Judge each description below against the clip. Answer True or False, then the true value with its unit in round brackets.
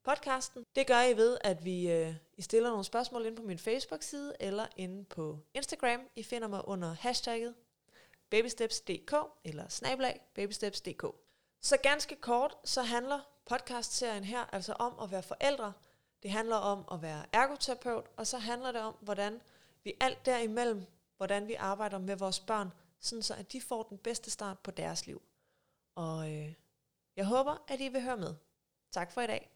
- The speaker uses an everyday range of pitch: True (4.1 semitones)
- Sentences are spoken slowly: False (170 wpm)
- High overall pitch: True (225 Hz)